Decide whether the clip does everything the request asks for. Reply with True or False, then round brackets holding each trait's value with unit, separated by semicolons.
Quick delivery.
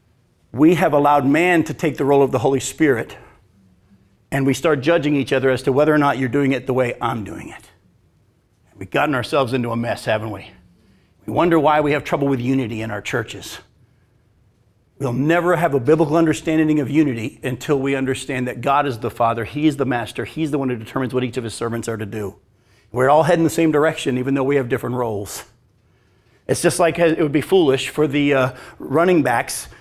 True (215 wpm)